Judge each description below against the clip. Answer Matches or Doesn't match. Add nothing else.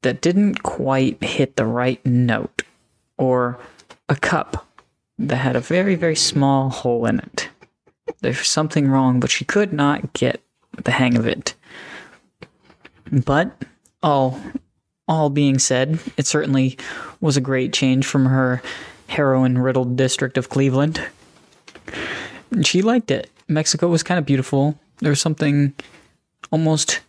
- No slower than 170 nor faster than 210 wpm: Doesn't match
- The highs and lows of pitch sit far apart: Doesn't match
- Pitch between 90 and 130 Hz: Doesn't match